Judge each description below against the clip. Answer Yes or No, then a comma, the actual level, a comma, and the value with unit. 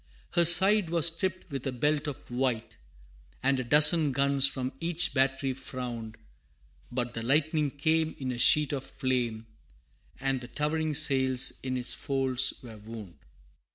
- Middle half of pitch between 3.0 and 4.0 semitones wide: Yes, average, 3.4 semitones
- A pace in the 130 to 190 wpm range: Yes, average, 155 wpm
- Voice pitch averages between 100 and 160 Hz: Yes, low, 135 Hz